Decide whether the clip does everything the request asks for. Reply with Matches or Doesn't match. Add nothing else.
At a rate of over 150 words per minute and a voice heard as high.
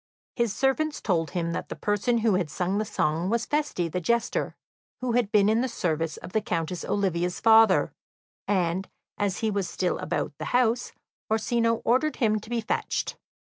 Matches